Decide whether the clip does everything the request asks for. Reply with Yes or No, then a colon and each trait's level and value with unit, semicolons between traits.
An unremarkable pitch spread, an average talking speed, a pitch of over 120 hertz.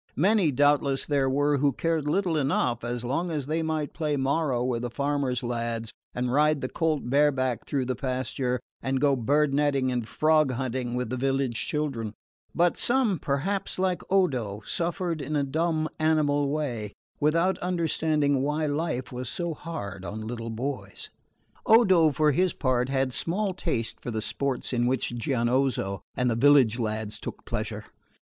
Yes: average, 4.0 semitones; average, 165 wpm; medium, 140 Hz